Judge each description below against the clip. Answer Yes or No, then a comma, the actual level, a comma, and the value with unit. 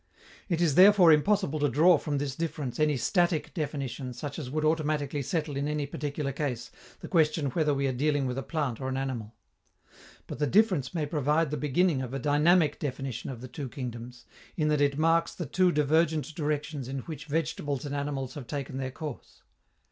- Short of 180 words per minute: No, average, 195 wpm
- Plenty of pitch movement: No, average, 2.7 semitones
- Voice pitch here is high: No, medium, 145 Hz